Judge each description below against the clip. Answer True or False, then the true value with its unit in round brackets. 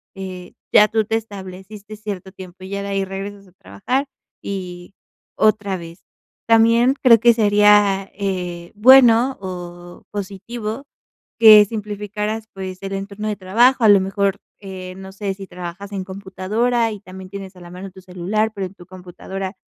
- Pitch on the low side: False (200 Hz)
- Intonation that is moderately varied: False (2.3 semitones)